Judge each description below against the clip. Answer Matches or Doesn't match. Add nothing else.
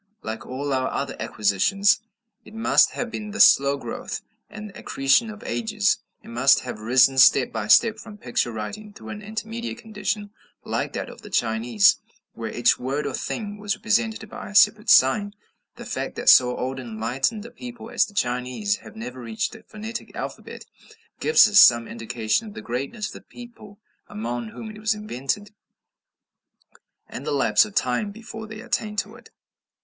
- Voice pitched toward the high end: Matches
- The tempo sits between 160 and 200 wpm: Matches